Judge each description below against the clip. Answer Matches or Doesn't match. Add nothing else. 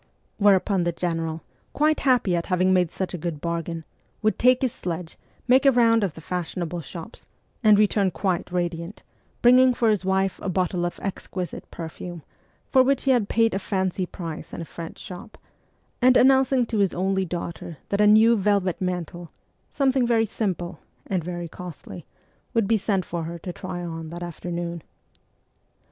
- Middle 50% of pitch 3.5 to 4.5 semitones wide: Matches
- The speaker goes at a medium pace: Matches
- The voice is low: Doesn't match